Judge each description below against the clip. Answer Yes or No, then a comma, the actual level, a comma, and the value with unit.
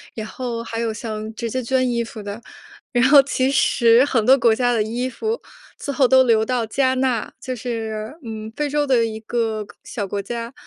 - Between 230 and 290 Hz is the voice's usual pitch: Yes, high, 235 Hz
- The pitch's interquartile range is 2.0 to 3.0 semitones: Yes, average, 2.7 semitones